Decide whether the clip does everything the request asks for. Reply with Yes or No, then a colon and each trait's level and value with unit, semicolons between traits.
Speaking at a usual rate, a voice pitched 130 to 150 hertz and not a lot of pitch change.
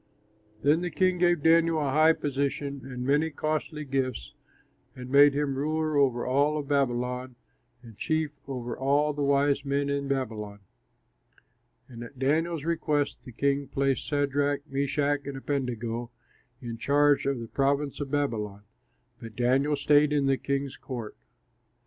Yes: average, 150 wpm; medium, 140 Hz; narrow, 2.2 semitones